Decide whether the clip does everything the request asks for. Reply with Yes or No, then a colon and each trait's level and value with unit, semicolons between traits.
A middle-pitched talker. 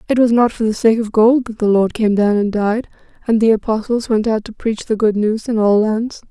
No: high, 220 Hz